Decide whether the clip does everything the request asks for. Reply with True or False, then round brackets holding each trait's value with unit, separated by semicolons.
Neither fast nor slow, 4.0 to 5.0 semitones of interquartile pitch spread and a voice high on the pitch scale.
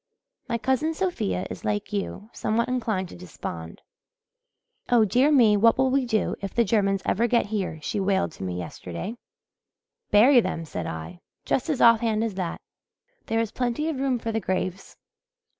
True (175 wpm; 4.5 semitones; 220 Hz)